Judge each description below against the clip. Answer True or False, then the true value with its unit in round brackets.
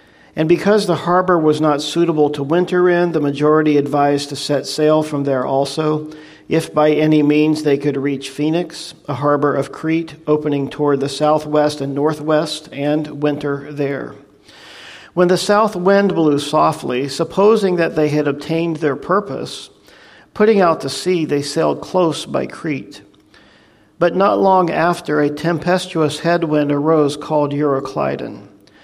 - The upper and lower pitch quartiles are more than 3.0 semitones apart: False (2.6 semitones)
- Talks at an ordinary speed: True (150 wpm)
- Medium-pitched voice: True (155 Hz)